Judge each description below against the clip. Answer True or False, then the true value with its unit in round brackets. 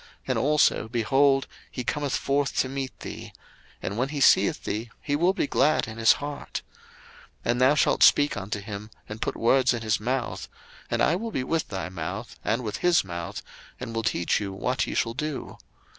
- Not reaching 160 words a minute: False (200 wpm)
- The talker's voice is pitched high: False (125 Hz)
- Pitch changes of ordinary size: True (4.8 semitones)